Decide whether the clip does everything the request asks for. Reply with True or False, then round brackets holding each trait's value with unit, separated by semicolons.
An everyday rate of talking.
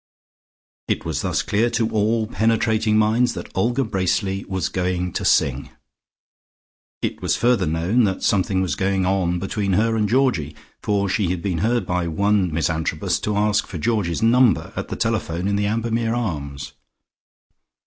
True (165 wpm)